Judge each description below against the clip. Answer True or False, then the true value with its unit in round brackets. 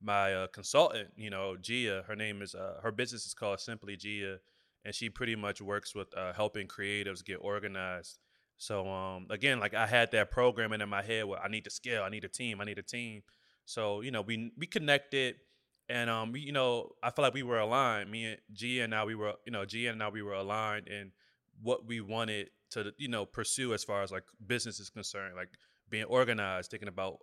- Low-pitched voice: True (105 Hz)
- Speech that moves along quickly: True (225 wpm)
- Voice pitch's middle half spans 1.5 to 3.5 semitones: True (2.7 semitones)